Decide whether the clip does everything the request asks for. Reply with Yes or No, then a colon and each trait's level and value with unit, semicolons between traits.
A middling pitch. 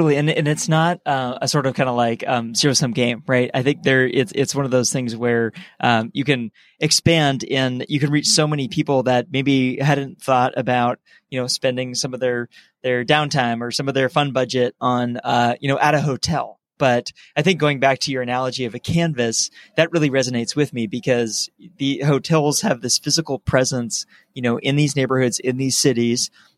No: low, 130 Hz